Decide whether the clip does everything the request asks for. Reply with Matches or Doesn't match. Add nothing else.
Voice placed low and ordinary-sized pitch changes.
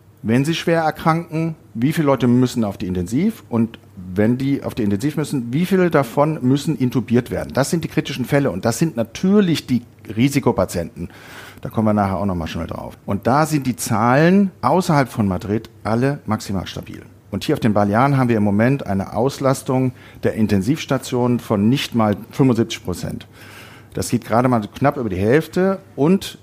Matches